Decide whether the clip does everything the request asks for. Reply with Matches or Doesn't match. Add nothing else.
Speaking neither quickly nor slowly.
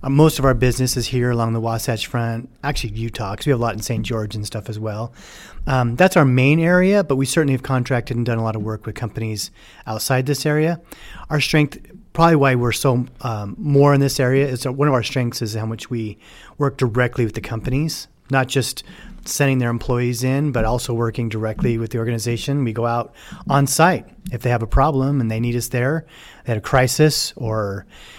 Doesn't match